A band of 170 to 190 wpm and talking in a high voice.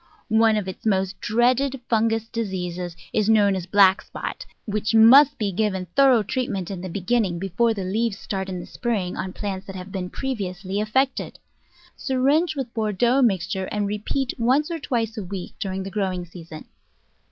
Yes: average, 175 wpm; high, 210 Hz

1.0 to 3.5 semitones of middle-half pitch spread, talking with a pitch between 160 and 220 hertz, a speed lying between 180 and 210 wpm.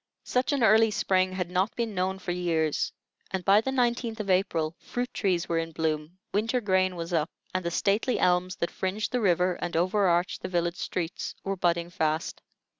Yes: average, 3.2 semitones; medium, 185 Hz; average, 190 wpm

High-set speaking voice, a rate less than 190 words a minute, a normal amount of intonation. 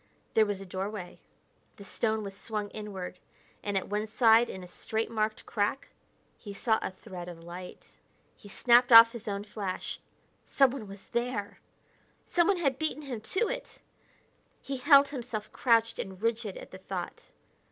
Yes: high, 215 Hz; average, 165 wpm; average, 3.4 semitones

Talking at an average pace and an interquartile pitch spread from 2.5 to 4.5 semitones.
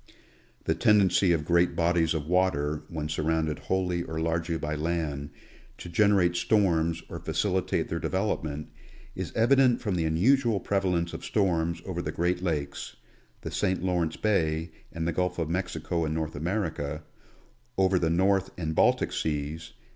Yes: average, 155 wpm; average, 2.8 semitones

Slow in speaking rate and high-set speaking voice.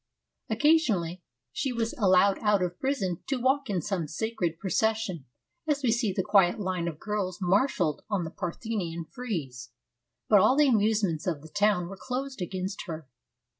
No: average, 170 wpm; high, 200 Hz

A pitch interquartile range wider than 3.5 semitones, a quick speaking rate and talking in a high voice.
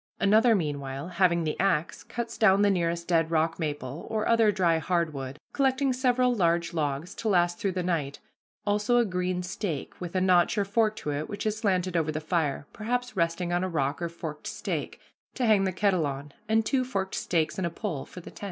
No: average, 4.5 semitones; fast, 215 wpm; medium, 180 Hz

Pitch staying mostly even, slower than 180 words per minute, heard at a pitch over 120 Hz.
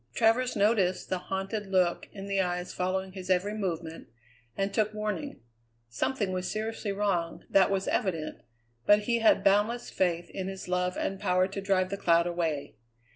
Yes: narrow, 2.3 semitones; average, 170 wpm; high, 190 Hz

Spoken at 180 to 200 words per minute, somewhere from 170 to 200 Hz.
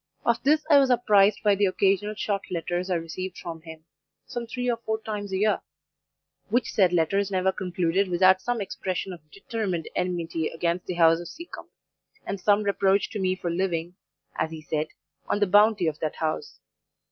Yes: average, 185 wpm; high, 190 Hz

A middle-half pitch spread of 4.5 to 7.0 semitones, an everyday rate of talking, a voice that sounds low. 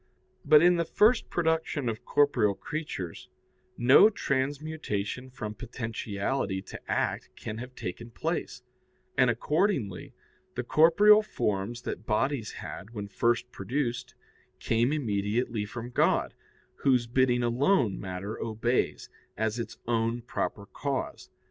No: average, 4.8 semitones; slow, 120 wpm; low, 120 Hz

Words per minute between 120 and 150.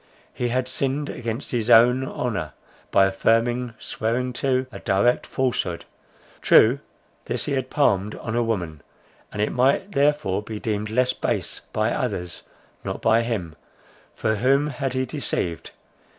Yes: slow, 135 wpm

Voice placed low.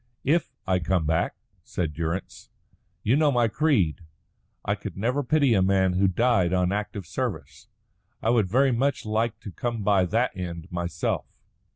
Yes: low, 100 Hz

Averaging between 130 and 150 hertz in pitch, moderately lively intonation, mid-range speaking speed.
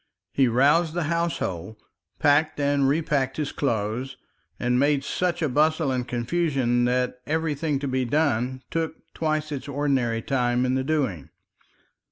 Yes: medium, 140 Hz; average, 3.7 semitones; average, 145 wpm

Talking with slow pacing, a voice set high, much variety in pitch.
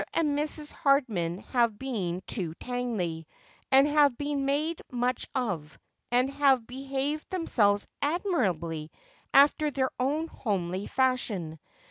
Yes: slow, 115 wpm; very high, 255 Hz; wide, 6.6 semitones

